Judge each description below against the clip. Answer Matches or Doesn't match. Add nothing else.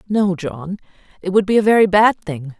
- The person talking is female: Matches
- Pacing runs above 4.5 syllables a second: Matches